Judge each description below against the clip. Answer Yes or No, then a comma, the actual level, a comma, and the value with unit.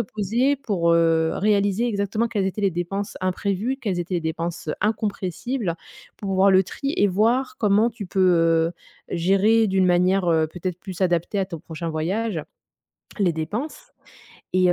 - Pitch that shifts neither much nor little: Yes, average, 3.6 semitones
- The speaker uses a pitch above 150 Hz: Yes, high, 190 Hz